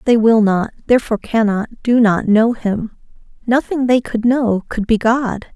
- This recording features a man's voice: No, female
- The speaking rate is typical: Yes, average, 175 wpm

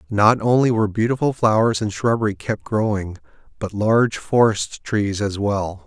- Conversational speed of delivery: Yes, average, 155 wpm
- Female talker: No, male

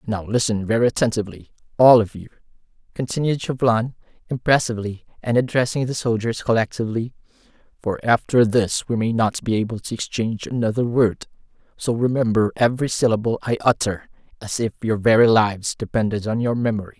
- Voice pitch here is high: No, low, 115 Hz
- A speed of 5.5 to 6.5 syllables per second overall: Yes, 5.9 syllables/s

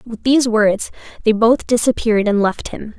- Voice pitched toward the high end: Yes, high, 220 Hz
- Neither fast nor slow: Yes, average, 180 wpm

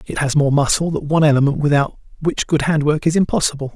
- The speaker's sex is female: No, male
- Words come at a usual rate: No, fast, 225 wpm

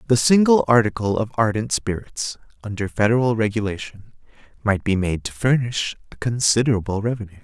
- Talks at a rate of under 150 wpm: Yes, slow, 135 wpm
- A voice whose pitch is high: No, low, 110 Hz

